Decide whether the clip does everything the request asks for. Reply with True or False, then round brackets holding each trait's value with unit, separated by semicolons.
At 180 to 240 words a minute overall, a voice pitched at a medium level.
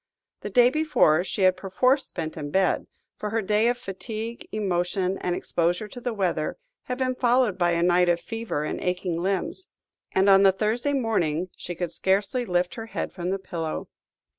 False (190 wpm; 195 Hz)